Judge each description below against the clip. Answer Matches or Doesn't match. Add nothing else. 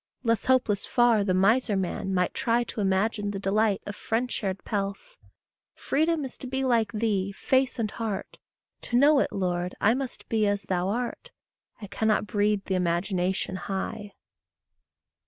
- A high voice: Matches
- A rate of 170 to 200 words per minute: Doesn't match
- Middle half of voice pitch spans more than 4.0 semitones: Doesn't match